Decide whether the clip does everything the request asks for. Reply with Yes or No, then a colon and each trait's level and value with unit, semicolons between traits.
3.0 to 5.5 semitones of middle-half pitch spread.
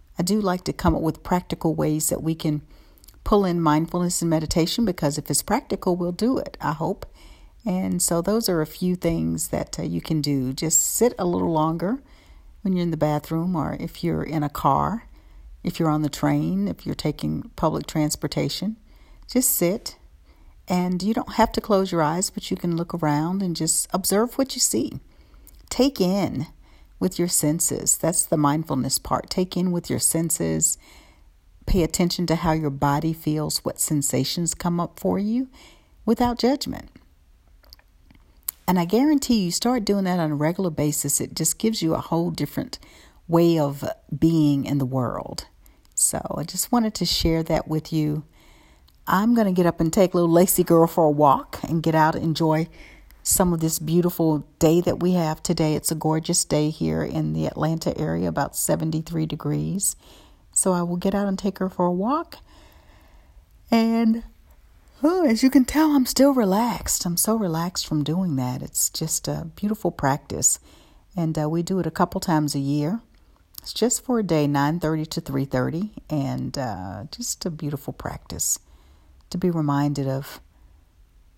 Yes: average, 4.0 semitones